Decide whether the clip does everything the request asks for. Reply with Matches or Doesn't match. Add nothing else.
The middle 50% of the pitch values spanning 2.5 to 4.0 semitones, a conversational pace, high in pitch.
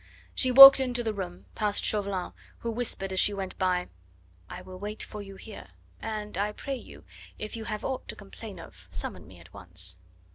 Matches